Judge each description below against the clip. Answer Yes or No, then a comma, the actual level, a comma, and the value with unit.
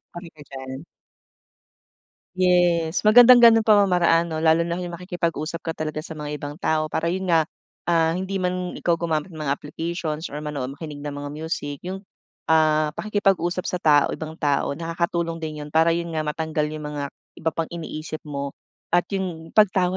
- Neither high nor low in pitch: Yes, medium, 165 Hz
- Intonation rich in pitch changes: No, narrow, 2.6 semitones